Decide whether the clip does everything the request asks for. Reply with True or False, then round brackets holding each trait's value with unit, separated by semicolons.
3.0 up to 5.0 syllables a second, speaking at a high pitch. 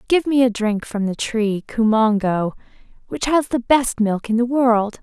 True (4.2 syllables/s; 230 Hz)